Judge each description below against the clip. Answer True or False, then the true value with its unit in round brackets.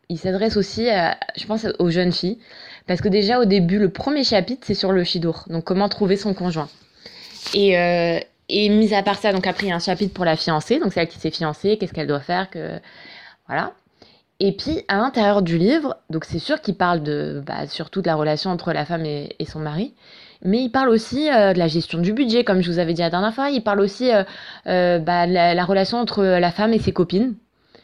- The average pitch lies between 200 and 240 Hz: False (190 Hz)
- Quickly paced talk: True (240 wpm)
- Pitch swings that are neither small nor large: True (3.4 semitones)